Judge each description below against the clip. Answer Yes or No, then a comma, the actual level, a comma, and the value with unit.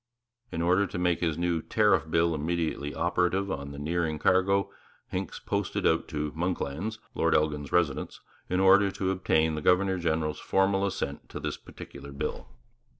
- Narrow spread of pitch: No, average, 3.2 semitones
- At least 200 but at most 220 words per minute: No, average, 160 wpm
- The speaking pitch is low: Yes, very low, 85 Hz